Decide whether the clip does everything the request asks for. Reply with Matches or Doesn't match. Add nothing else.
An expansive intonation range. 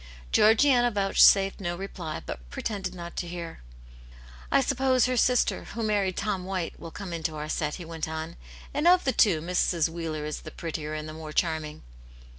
Doesn't match